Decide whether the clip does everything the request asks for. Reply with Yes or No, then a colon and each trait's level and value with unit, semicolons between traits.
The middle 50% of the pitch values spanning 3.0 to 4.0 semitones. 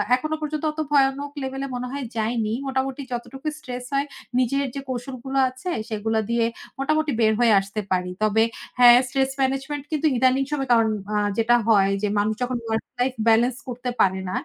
Yes: average, 3.4 semitones